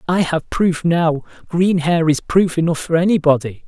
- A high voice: No, medium, 165 Hz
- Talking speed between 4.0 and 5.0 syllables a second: Yes, 4.6 syllables/s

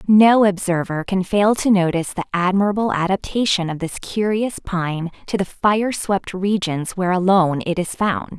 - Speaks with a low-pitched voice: No, high, 190 Hz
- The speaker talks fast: No, average, 165 wpm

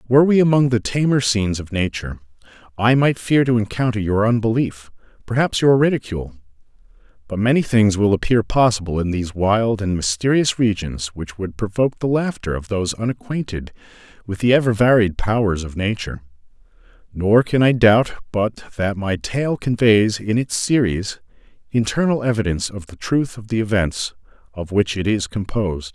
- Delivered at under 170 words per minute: Yes, average, 160 wpm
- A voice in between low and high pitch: No, low, 110 Hz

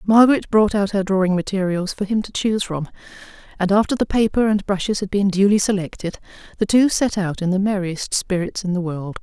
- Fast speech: Yes, fast, 210 wpm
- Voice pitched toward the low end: No, high, 195 Hz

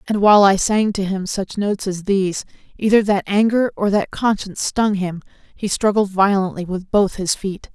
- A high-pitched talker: Yes, high, 200 Hz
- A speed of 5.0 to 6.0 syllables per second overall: Yes, 5.1 syllables/s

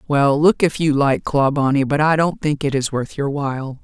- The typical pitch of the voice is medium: Yes, medium, 145 Hz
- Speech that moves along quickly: Yes, fast, 235 wpm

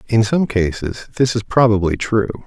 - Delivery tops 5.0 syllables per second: No, 4.9 syllables/s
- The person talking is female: No, male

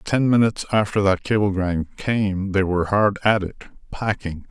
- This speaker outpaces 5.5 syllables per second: No, 5.0 syllables/s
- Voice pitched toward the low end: Yes, low, 100 Hz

